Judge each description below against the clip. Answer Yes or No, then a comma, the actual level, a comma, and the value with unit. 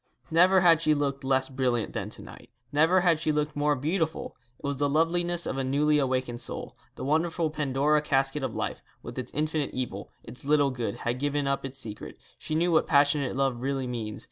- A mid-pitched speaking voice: Yes, medium, 145 Hz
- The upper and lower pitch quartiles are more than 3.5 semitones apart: No, average, 2.8 semitones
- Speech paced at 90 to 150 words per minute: No, fast, 205 wpm